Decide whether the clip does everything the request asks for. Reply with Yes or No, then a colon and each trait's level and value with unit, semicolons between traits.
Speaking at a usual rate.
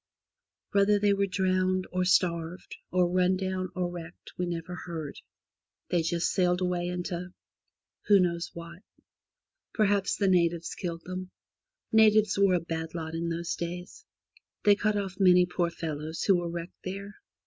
Yes: average, 160 wpm